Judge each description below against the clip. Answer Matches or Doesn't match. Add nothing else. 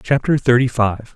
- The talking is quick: Doesn't match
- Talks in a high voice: Doesn't match